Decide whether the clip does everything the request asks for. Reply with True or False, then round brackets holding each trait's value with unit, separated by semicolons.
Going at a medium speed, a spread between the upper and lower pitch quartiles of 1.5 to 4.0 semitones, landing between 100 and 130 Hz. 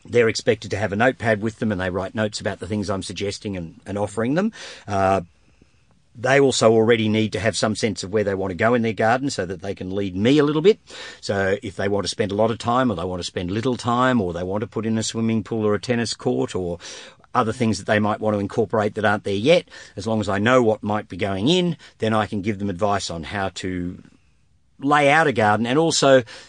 False (265 wpm; 2.9 semitones; 110 Hz)